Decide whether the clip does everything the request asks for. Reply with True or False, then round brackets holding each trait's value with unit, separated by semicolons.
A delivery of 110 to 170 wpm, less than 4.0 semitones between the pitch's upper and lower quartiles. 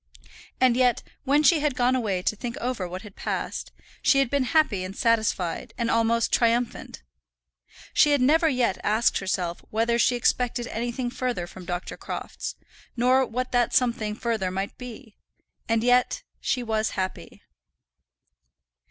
True (150 wpm; 2.9 semitones)